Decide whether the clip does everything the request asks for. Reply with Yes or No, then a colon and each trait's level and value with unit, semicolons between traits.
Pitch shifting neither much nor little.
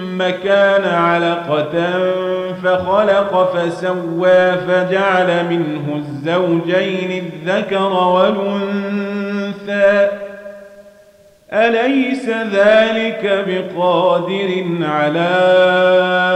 No: narrow, 1.9 semitones